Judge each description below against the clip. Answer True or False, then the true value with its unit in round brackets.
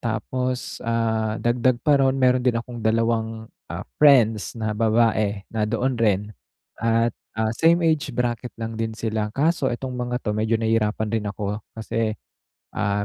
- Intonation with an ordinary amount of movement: False (2.1 semitones)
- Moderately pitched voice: False (115 Hz)